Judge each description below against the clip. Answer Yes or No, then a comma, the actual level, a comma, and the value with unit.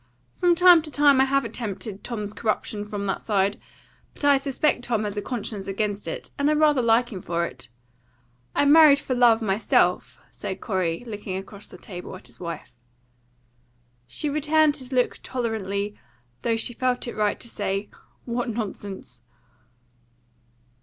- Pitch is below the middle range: No, high, 225 Hz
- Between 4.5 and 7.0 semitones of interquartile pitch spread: Yes, average, 5.0 semitones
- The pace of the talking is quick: No, average, 160 wpm